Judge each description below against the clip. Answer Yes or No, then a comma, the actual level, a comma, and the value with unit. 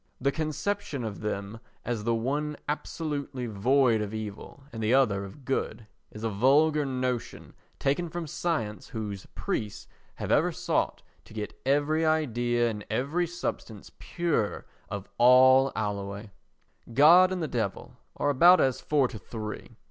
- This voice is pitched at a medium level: No, low, 125 Hz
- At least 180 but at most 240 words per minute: No, average, 150 wpm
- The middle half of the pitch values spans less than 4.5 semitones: No, wide, 5.5 semitones